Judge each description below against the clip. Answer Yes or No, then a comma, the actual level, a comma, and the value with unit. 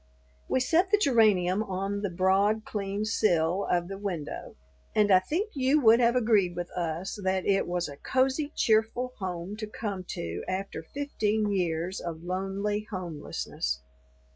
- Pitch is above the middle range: Yes, high, 195 Hz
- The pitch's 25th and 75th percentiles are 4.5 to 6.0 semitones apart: No, average, 3.6 semitones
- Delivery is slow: No, average, 155 wpm